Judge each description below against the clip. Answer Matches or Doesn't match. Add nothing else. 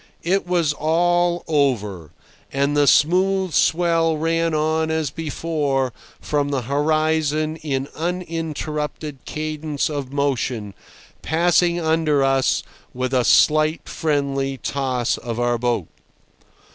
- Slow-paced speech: Matches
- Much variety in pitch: Doesn't match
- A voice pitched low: Doesn't match